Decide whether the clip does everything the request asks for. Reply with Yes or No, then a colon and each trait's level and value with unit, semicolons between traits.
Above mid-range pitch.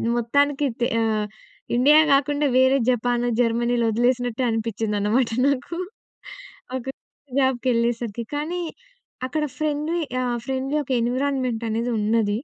Yes: high, 245 Hz